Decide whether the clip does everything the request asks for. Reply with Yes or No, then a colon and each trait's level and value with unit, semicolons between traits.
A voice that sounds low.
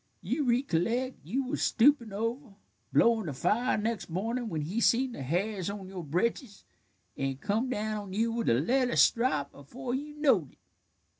No: high, 225 Hz